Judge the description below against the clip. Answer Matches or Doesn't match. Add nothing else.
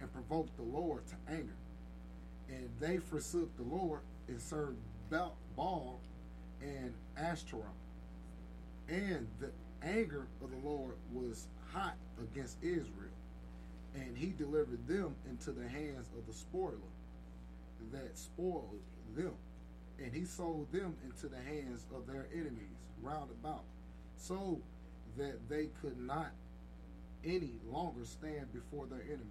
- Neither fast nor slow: Doesn't match